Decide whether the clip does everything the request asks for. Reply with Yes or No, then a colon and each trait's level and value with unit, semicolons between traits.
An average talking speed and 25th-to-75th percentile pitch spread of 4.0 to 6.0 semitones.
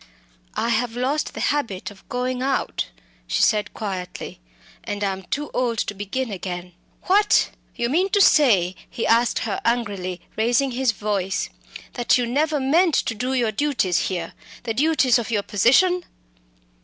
Yes: average, 160 wpm; average, 4.7 semitones